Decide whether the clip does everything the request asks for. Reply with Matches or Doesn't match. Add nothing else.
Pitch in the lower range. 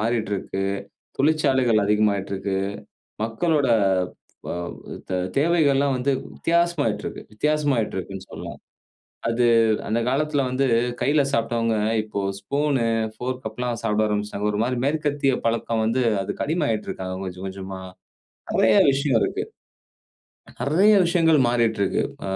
Matches